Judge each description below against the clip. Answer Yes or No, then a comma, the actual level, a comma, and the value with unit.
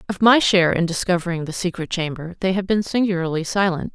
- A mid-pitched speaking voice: Yes, medium, 180 Hz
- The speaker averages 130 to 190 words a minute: No, average, 200 wpm